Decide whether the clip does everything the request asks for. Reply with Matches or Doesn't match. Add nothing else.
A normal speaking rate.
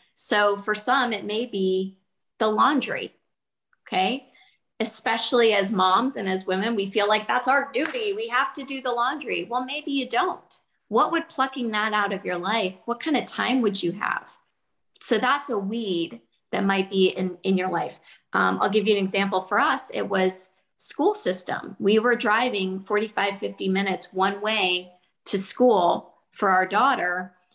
Matches